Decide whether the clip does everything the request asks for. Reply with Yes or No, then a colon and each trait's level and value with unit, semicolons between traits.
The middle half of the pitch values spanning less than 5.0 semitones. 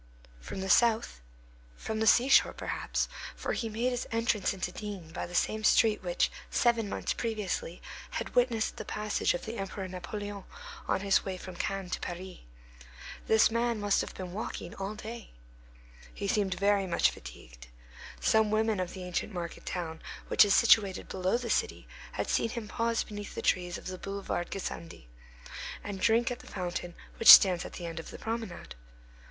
Yes: average, 3.4 semitones